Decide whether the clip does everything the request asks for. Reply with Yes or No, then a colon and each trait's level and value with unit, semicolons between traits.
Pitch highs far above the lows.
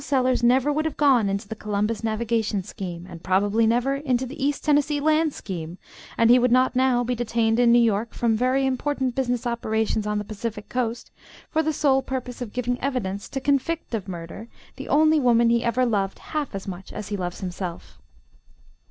No: average, 4.0 semitones